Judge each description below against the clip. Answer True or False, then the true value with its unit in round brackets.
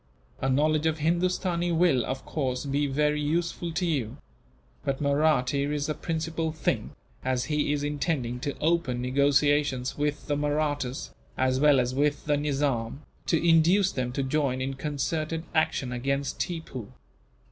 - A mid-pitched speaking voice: True (145 Hz)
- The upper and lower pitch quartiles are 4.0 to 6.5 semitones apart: False (3.0 semitones)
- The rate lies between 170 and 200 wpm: False (150 wpm)